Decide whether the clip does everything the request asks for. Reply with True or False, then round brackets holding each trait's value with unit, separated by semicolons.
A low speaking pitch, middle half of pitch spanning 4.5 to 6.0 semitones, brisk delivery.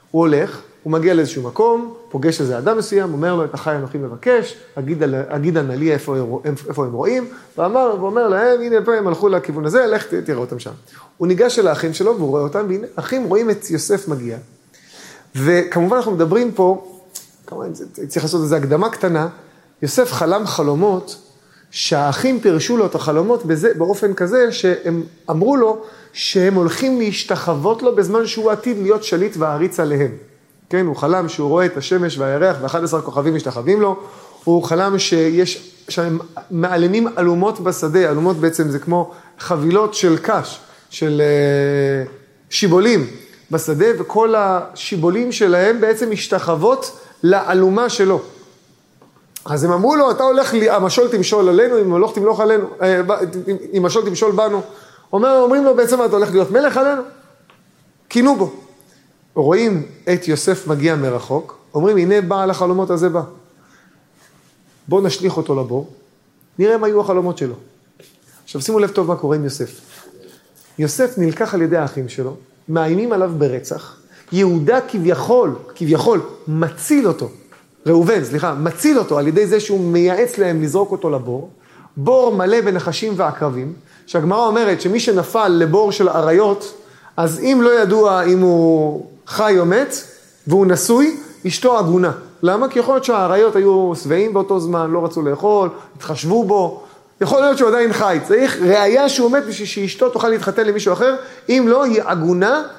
False (185 Hz; 5.2 semitones; 155 wpm)